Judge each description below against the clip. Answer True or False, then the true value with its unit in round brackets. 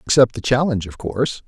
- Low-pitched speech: True (115 Hz)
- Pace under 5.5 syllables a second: False (6.3 syllables/s)